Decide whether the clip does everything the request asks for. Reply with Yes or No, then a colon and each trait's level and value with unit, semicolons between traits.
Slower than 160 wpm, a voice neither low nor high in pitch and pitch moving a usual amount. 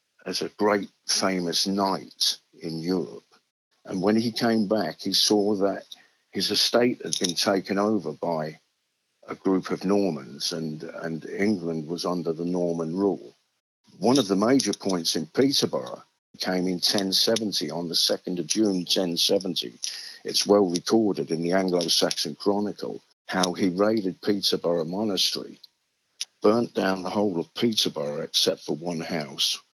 No: average, 145 wpm; very low, 95 Hz; average, 3.2 semitones